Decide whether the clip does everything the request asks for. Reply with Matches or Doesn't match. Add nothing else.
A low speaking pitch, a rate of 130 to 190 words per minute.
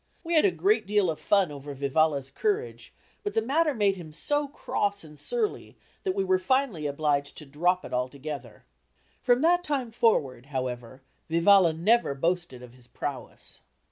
Doesn't match